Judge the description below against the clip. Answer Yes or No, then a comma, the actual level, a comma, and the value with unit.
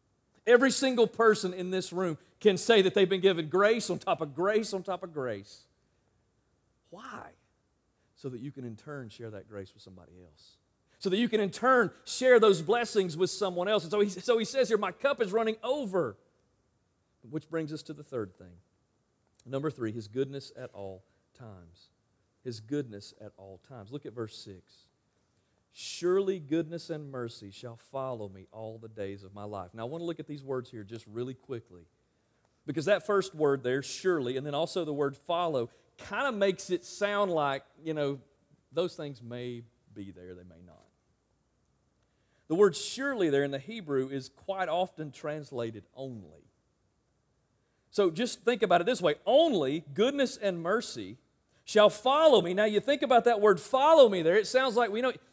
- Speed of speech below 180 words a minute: No, average, 190 wpm